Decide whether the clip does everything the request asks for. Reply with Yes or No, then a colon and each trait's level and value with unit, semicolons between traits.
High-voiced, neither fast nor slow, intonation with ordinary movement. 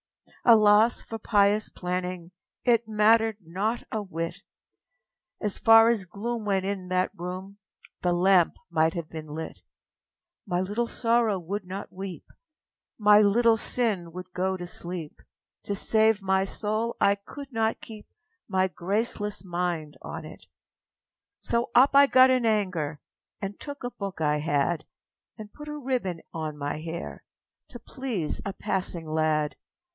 Yes: high, 195 Hz; average, 150 wpm; average, 4.1 semitones